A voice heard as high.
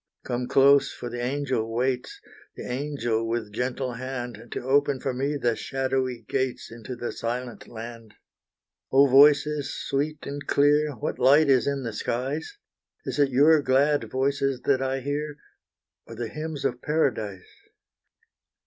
No: low, 130 Hz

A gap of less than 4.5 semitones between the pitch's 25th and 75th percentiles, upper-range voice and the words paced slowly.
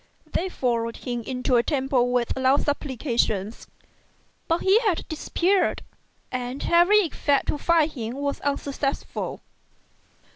No: average, 4.8 semitones; very high, 275 Hz; slow, 120 wpm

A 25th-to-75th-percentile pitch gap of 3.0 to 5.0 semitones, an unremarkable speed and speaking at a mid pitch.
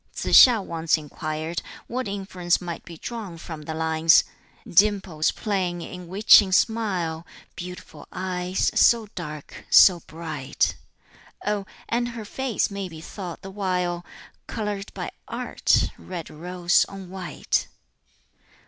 No: average, 3.3 semitones; slow, 125 wpm; medium, 180 Hz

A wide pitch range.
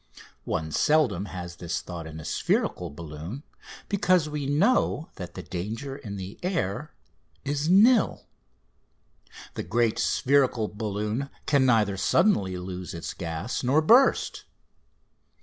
Yes: wide, 8.4 semitones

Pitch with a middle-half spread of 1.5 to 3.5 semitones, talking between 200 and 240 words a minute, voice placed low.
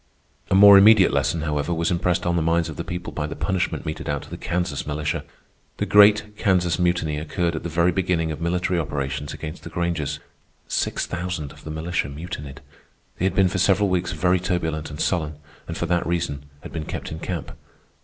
Yes: average, 2.7 semitones; fast, 205 wpm; very low, 85 Hz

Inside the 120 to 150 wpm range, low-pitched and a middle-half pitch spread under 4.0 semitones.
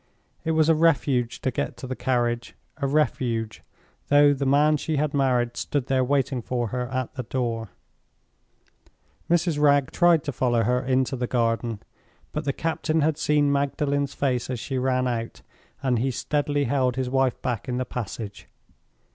No: average, 170 wpm; low, 130 Hz; average, 2.7 semitones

